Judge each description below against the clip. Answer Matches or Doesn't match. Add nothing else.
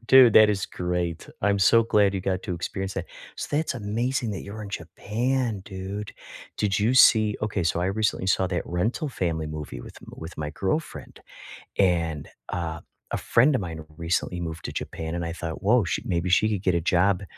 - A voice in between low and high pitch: Doesn't match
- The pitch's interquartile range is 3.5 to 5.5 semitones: Matches